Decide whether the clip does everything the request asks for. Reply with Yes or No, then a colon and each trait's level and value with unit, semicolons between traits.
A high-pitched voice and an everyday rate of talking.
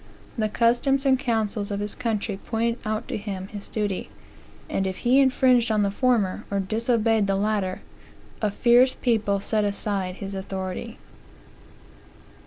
Yes: high, 215 Hz; average, 150 wpm